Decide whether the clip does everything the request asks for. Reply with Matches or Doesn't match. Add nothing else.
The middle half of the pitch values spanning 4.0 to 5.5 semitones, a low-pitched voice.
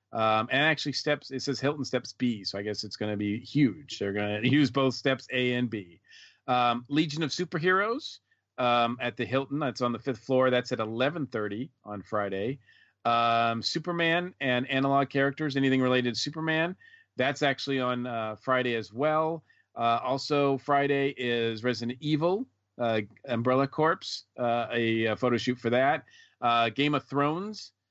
Doesn't match